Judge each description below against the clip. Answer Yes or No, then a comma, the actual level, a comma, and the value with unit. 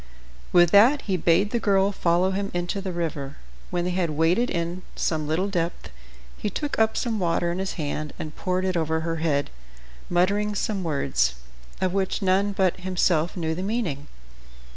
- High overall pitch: No, medium, 180 Hz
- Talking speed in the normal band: Yes, average, 180 wpm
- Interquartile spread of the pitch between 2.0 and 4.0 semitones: Yes, average, 3.2 semitones